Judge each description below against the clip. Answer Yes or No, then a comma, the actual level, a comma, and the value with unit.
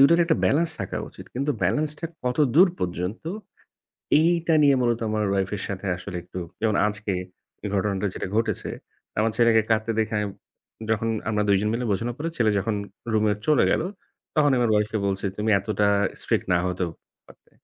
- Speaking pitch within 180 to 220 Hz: No, low, 110 Hz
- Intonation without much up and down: No, average, 4.1 semitones